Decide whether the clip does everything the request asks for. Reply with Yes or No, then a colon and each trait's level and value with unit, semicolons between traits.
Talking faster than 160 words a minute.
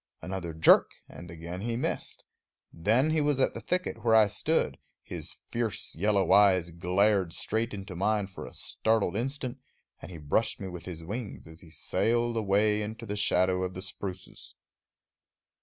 Yes: average, 170 wpm